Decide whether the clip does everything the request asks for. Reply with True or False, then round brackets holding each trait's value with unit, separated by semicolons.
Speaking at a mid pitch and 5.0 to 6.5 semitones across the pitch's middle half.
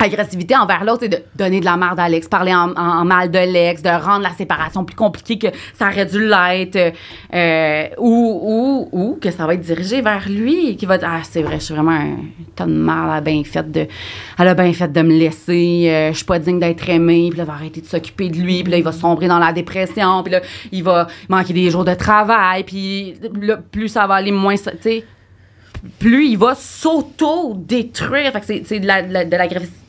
False (180 Hz; 3.4 semitones)